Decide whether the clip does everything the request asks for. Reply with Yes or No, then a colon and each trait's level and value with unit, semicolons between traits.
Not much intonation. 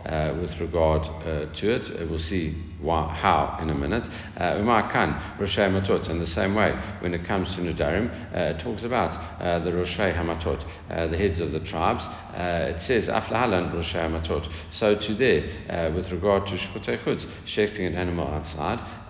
No: average, 3.2 semitones